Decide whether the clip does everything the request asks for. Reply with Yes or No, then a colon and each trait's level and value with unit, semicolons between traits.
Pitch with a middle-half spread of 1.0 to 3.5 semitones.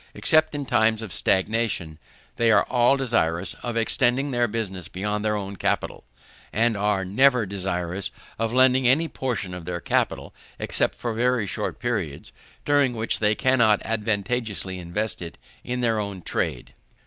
No: average, 4.1 semitones